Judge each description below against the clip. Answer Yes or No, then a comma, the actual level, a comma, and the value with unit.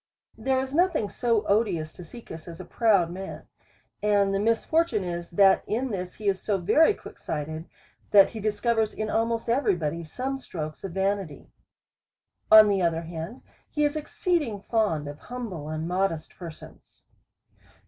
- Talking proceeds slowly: No, average, 160 wpm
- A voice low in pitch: No, high, 200 Hz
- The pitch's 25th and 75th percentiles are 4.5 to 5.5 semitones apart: Yes, average, 5.2 semitones